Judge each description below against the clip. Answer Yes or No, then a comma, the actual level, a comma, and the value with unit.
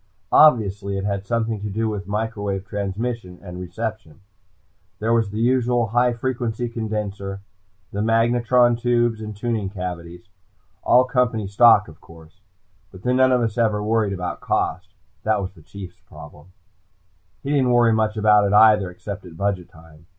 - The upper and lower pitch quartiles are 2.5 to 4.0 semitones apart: Yes, average, 3.2 semitones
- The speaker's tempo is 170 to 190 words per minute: No, average, 160 wpm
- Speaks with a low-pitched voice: Yes, low, 105 Hz